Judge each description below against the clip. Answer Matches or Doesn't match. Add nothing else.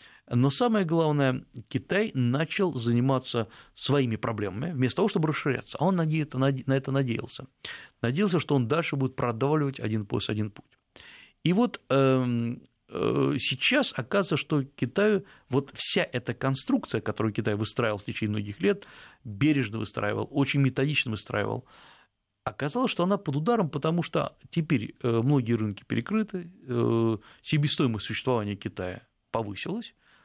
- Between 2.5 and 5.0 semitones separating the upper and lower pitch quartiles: Doesn't match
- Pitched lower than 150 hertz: Matches